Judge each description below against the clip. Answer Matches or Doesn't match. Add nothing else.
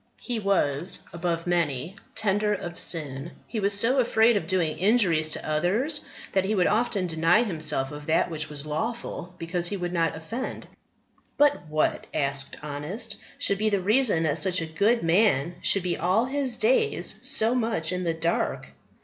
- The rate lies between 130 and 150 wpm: Doesn't match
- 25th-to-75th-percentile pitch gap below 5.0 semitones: Doesn't match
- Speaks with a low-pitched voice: Doesn't match